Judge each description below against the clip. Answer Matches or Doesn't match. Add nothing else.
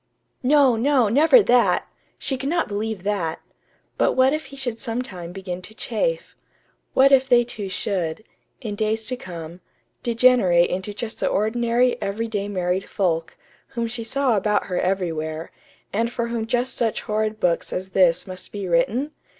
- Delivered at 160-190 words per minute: Matches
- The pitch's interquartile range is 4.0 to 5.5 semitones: Matches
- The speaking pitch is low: Doesn't match